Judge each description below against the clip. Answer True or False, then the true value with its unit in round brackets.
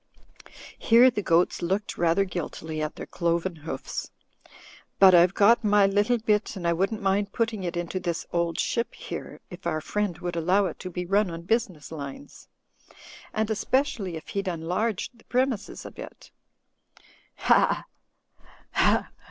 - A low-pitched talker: False (190 Hz)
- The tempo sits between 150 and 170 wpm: True (155 wpm)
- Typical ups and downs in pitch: True (3.8 semitones)